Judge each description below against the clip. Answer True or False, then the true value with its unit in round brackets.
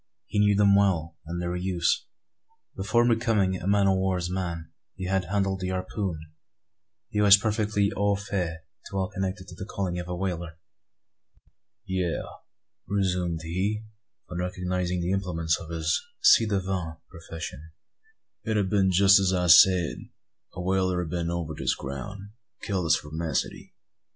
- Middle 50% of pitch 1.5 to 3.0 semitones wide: True (2.4 semitones)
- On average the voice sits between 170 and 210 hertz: False (95 Hz)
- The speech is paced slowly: False (155 wpm)